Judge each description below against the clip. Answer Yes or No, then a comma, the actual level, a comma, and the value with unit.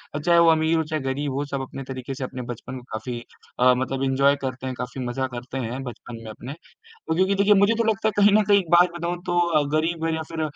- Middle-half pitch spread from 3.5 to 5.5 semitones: Yes, average, 5.0 semitones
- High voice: No, medium, 140 Hz